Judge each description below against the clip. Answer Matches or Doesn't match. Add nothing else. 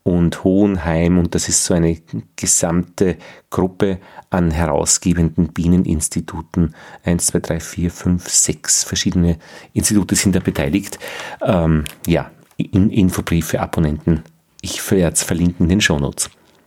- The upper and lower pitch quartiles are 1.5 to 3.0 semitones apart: Matches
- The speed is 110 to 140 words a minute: Matches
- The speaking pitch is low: Matches